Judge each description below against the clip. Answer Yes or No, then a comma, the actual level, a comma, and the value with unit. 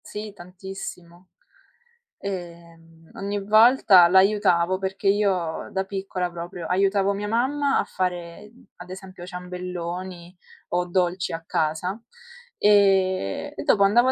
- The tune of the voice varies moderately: No, narrow, 2.3 semitones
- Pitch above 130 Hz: Yes, medium, 185 Hz